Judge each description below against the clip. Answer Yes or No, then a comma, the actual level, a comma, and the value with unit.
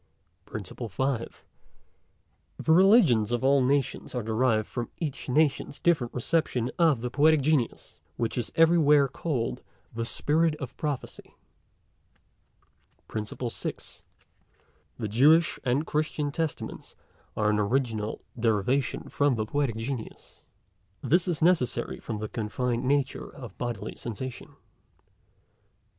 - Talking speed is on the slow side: Yes, slow, 120 wpm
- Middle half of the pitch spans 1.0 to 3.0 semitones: No, average, 4.5 semitones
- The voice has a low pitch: Yes, low, 130 Hz